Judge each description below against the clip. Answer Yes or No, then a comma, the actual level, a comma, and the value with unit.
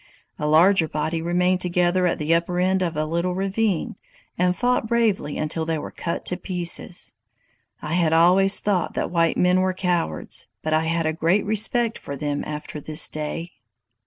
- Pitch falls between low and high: Yes, medium, 175 Hz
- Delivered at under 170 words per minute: No, average, 180 wpm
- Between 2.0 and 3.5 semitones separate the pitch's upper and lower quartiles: Yes, average, 2.8 semitones